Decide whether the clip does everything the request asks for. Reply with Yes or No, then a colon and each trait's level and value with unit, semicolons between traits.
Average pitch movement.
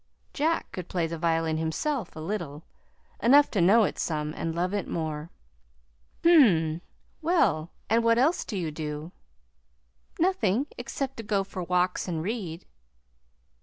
No: wide, 6.3 semitones